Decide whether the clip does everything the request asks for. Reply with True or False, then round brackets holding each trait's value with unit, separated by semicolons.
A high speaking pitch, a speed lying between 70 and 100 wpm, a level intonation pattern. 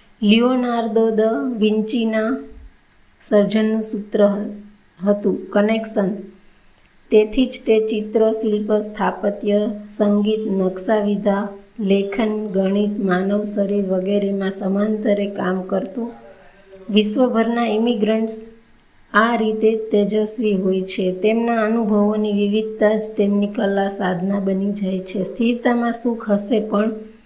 True (210 Hz; 95 wpm; 1.7 semitones)